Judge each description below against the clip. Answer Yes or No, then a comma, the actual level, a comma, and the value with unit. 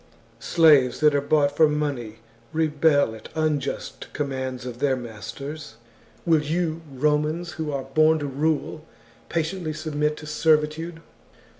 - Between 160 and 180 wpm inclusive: No, slow, 135 wpm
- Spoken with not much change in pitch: Yes, narrow, 2.3 semitones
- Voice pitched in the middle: Yes, medium, 150 Hz